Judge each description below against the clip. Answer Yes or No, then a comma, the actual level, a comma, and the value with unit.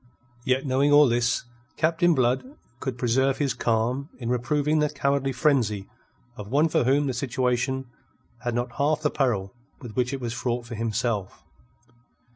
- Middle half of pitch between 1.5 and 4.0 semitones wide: Yes, average, 3.0 semitones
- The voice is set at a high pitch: No, low, 130 Hz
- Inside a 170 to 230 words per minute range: No, average, 160 wpm